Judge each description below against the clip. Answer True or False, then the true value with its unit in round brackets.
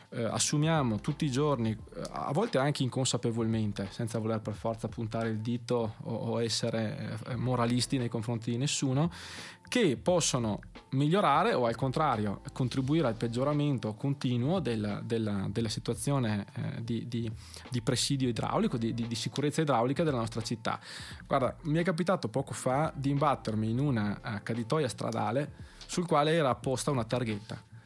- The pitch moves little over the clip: False (3.9 semitones)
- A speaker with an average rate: True (145 wpm)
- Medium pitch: False (120 Hz)